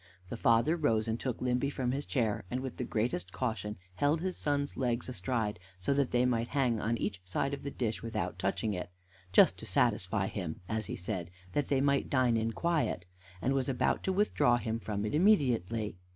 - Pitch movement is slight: No, average, 4.3 semitones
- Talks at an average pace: No, fast, 210 wpm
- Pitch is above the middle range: No, low, 120 Hz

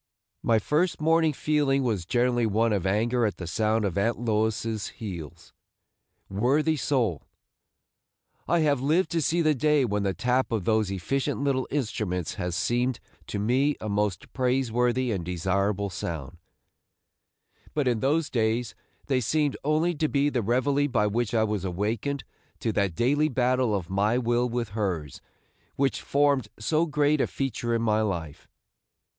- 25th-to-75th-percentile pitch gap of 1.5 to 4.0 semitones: No, average, 5.3 semitones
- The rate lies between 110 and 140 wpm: No, average, 160 wpm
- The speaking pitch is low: Yes, low, 120 Hz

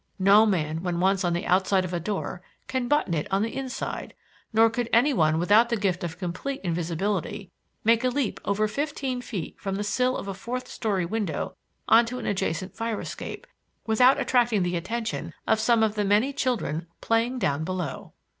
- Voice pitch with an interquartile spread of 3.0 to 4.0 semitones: No, average, 4.7 semitones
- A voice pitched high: Yes, high, 210 Hz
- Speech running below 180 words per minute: No, average, 195 wpm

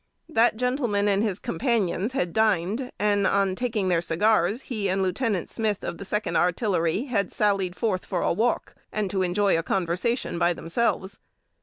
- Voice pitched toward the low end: No, high, 200 Hz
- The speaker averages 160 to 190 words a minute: Yes, average, 165 wpm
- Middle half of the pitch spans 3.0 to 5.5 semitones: Yes, average, 3.5 semitones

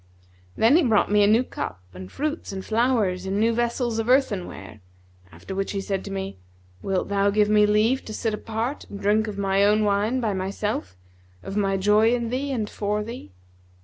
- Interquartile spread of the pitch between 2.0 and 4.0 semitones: Yes, average, 2.8 semitones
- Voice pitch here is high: Yes, high, 210 Hz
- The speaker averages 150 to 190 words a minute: No, average, 200 wpm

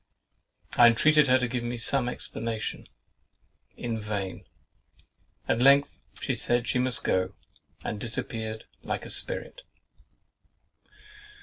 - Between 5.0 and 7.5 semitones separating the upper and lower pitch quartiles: No, narrow, 2.5 semitones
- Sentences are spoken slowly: Yes, slow, 115 wpm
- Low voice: Yes, low, 120 Hz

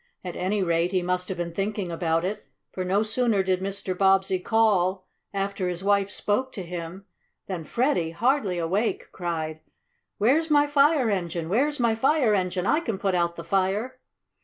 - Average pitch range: Yes, average, 3.7 semitones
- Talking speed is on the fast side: No, average, 175 wpm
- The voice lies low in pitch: No, high, 195 Hz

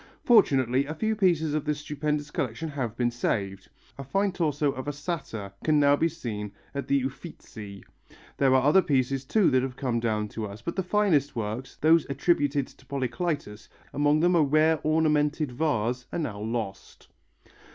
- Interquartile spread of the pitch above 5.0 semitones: No, average, 4.3 semitones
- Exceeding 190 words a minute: No, average, 175 wpm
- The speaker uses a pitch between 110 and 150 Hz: Yes, medium, 140 Hz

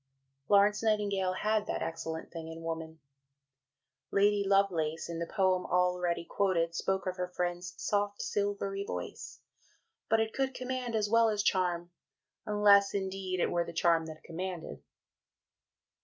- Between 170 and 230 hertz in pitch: Yes, medium, 185 Hz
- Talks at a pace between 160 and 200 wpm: No, average, 145 wpm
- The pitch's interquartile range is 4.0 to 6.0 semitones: No, average, 3.3 semitones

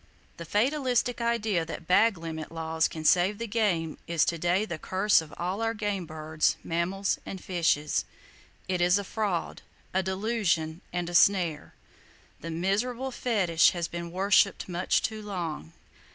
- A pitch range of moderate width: Yes, average, 3.9 semitones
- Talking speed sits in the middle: Yes, average, 155 wpm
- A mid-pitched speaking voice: Yes, medium, 180 Hz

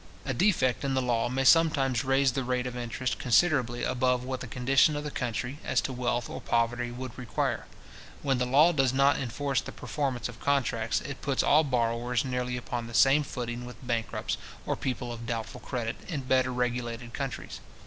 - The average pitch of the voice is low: Yes, low, 125 Hz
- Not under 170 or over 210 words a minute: Yes, average, 190 wpm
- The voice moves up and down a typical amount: No, narrow, 2.0 semitones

